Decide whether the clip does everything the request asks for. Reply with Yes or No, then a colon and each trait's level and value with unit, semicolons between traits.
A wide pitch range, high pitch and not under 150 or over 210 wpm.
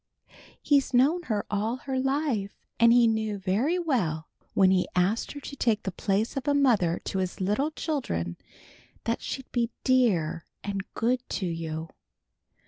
Yes: wide, 5.7 semitones; high, 220 Hz; average, 160 wpm